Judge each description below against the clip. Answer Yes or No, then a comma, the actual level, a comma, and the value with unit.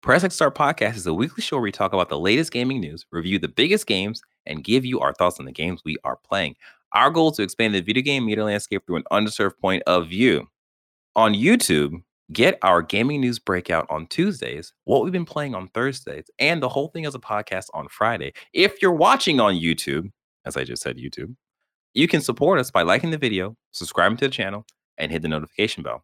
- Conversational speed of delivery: No, fast, 225 wpm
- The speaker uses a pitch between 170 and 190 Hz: No, low, 105 Hz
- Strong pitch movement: Yes, wide, 7.2 semitones